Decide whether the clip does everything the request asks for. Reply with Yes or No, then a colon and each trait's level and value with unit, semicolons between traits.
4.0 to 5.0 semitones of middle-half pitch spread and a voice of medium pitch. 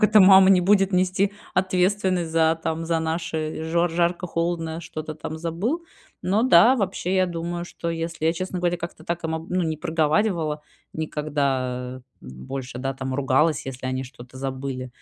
No: average, 3.4 semitones; medium, 165 Hz